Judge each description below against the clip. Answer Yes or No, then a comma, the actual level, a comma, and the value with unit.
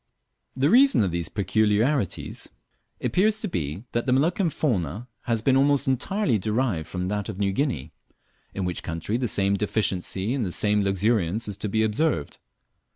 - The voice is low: Yes, low, 110 Hz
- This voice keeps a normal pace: Yes, average, 170 wpm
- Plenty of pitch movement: Yes, wide, 5.7 semitones